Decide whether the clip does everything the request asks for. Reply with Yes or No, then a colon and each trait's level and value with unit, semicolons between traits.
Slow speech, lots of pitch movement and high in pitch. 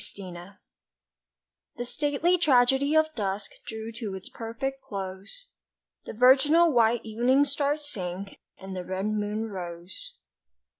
Yes: slow, 120 wpm; wide, 6.3 semitones; high, 225 Hz